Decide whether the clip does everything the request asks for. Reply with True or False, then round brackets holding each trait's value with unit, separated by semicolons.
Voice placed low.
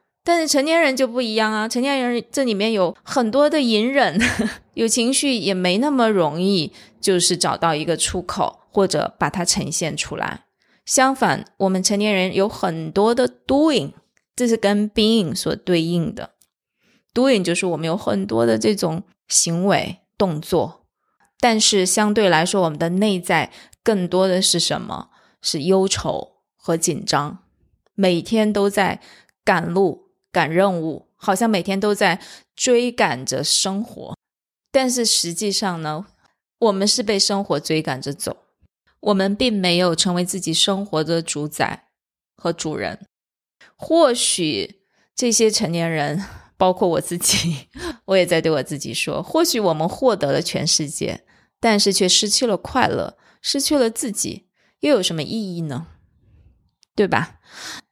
False (195 Hz)